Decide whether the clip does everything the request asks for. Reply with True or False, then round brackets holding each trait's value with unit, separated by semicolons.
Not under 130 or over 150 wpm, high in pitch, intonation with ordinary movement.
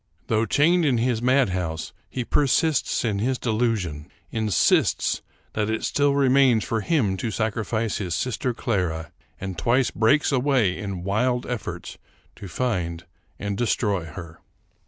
False (140 wpm; 110 Hz; 4.6 semitones)